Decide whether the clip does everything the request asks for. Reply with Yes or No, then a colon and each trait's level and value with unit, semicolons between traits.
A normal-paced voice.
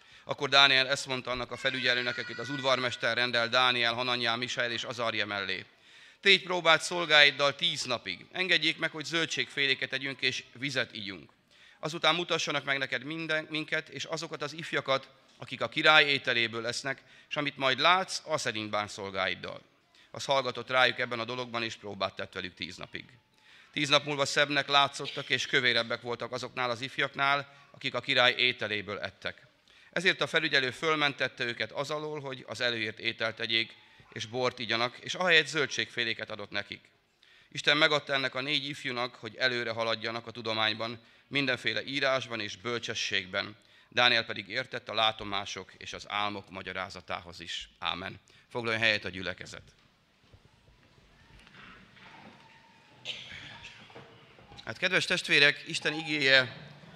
Yes: average, 145 wpm